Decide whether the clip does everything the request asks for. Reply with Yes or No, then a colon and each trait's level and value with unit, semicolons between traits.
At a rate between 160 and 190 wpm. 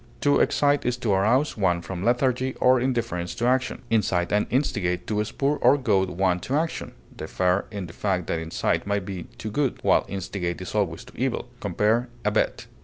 Yes: average, 185 wpm